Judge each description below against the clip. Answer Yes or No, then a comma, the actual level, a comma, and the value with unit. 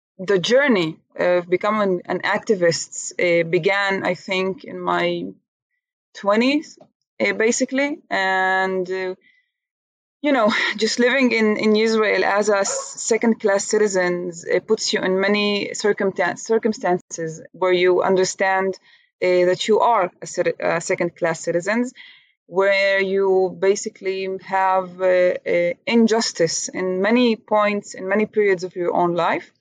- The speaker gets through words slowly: Yes, slow, 115 wpm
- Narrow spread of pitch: No, average, 3.5 semitones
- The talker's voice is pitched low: No, high, 195 Hz